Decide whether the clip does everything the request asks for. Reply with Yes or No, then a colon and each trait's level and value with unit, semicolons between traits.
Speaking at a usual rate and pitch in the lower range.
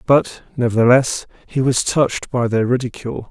Yes: average, 145 wpm; low, 125 Hz